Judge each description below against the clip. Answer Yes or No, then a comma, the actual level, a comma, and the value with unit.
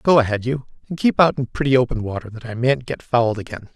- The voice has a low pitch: Yes, low, 125 Hz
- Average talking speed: No, fast, 255 wpm